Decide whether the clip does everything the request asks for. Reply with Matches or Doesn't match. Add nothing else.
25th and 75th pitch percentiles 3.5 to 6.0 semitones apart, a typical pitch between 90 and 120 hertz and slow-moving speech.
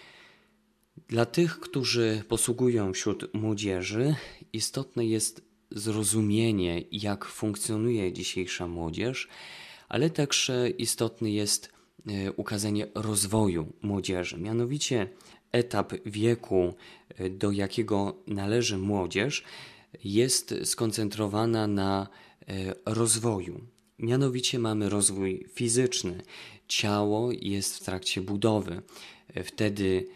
Doesn't match